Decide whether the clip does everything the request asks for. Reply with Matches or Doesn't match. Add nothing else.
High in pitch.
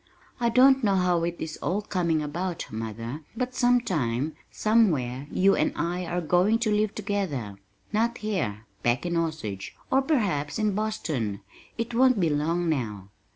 Doesn't match